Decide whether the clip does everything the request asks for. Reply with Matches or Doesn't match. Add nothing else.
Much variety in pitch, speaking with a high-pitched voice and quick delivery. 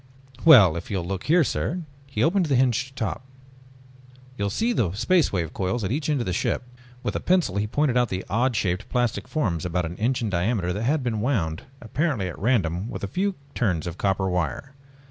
Doesn't match